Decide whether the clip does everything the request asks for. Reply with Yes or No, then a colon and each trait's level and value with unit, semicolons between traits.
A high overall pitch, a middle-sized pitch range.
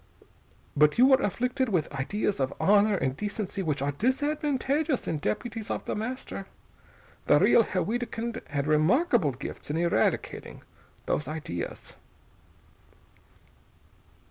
No: high, 205 Hz; wide, 8.5 semitones